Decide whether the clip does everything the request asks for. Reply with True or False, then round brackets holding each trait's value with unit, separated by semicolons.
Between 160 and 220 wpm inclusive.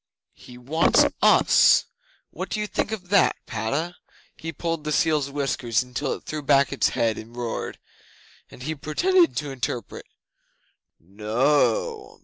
False (140 wpm)